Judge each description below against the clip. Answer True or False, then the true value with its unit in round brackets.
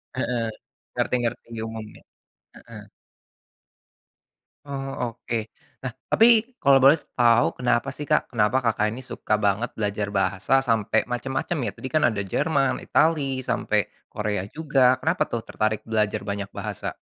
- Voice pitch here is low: True (120 Hz)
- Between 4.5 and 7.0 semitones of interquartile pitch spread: False (4.1 semitones)